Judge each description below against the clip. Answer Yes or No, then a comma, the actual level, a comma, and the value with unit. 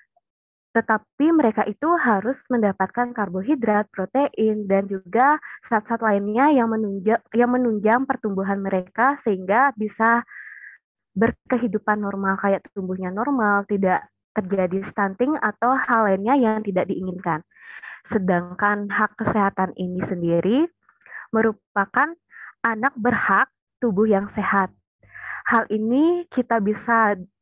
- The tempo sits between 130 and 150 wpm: No, average, 105 wpm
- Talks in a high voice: Yes, high, 215 Hz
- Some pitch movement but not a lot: Yes, average, 3.6 semitones